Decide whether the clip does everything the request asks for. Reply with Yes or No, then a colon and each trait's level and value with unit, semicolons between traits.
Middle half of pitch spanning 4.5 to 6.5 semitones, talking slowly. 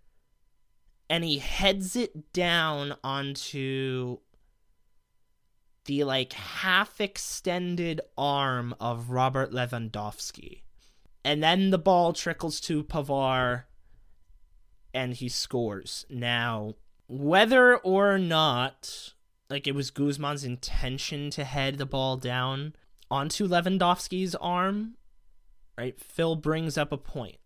Yes: average, 5.1 semitones; slow, 105 wpm